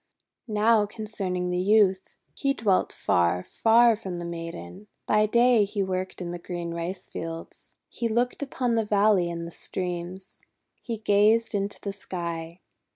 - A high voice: Yes, high, 195 Hz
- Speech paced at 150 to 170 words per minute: Yes, average, 155 wpm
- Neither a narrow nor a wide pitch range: Yes, average, 3.9 semitones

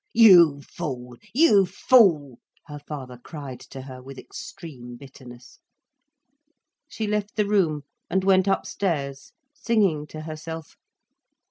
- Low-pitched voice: No, medium, 155 Hz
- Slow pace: Yes, slow, 115 wpm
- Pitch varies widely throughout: Yes, wide, 6.2 semitones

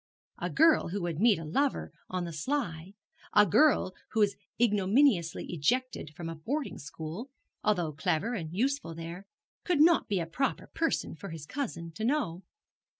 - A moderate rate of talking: Yes, average, 165 wpm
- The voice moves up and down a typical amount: No, wide, 7.7 semitones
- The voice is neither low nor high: No, high, 195 Hz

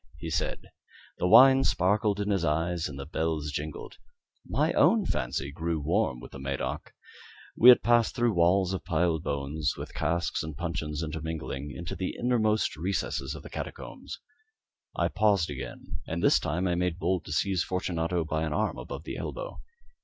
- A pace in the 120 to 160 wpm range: No, average, 170 wpm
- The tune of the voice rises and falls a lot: No, average, 4.2 semitones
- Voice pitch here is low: Yes, very low, 85 Hz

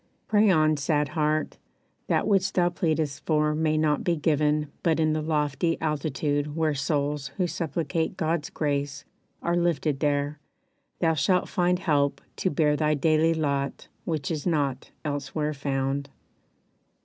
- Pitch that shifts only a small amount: Yes, narrow, 2.2 semitones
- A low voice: No, medium, 150 Hz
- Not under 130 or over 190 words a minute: Yes, average, 145 wpm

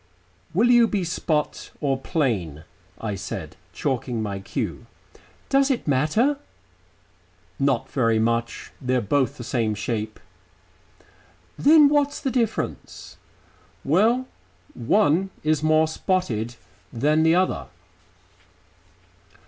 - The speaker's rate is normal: No, slow, 105 wpm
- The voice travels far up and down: Yes, wide, 8.9 semitones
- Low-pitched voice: No, medium, 145 Hz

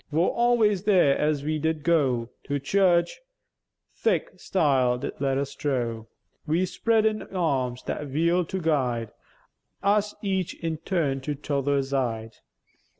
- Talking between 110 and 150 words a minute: Yes, slow, 135 wpm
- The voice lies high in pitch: No, medium, 150 Hz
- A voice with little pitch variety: No, average, 5.3 semitones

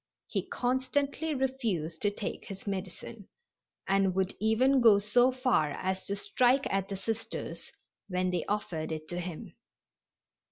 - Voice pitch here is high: Yes, high, 205 Hz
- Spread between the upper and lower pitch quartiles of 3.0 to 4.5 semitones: No, wide, 5.5 semitones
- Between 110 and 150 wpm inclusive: Yes, average, 145 wpm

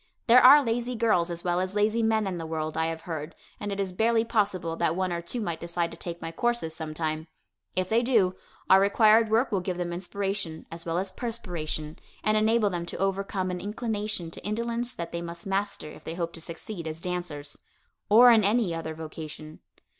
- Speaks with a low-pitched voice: No, medium, 185 Hz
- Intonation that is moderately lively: Yes, average, 4.5 semitones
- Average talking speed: No, fast, 210 wpm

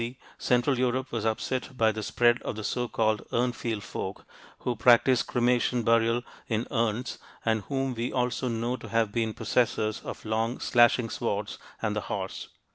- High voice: No, low, 120 Hz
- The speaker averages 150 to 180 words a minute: Yes, average, 170 wpm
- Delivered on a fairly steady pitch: Yes, narrow, 1.8 semitones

